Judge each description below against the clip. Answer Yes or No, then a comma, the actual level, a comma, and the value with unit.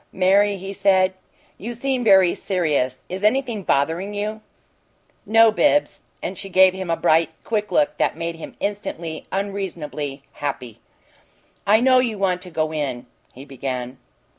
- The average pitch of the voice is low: No, high, 190 Hz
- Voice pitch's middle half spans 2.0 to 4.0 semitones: No, average, 4.8 semitones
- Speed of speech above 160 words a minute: No, average, 155 wpm